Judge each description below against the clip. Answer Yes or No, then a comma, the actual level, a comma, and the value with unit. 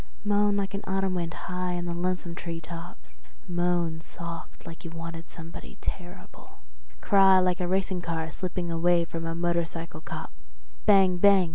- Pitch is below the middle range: No, medium, 175 Hz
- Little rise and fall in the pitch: Yes, narrow, 1.8 semitones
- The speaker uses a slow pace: No, average, 160 wpm